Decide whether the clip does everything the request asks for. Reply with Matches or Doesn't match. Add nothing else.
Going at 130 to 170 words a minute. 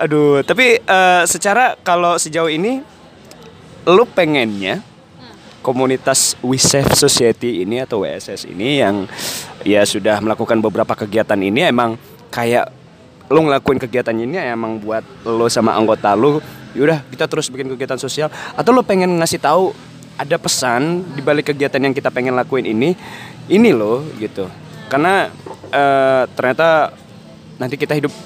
Matches